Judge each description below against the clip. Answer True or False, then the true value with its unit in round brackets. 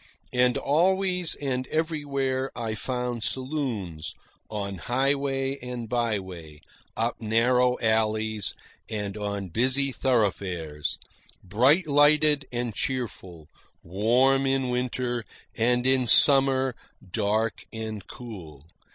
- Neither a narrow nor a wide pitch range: True (4.0 semitones)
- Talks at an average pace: False (100 wpm)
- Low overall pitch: True (120 Hz)